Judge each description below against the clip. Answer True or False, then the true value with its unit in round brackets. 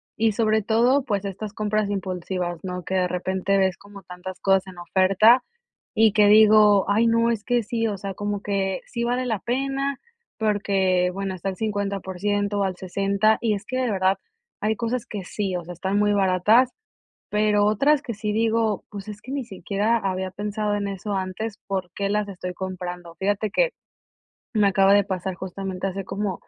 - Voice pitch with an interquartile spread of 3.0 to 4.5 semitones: False (2.4 semitones)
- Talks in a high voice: True (200 Hz)